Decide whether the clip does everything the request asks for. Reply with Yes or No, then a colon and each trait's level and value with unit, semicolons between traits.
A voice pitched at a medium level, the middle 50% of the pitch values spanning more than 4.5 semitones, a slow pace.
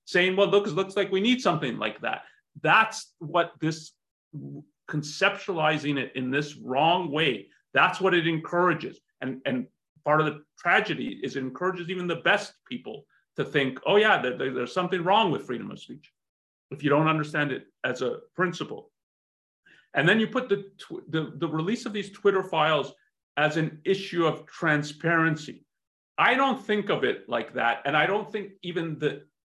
No: medium, 170 Hz; average, 4.9 semitones; average, 180 wpm